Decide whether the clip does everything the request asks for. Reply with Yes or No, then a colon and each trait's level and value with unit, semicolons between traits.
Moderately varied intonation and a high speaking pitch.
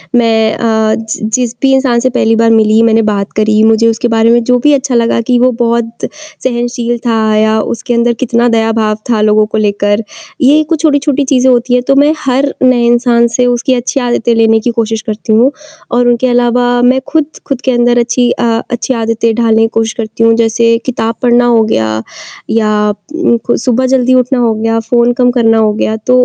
No: narrow, 1.8 semitones; high, 235 Hz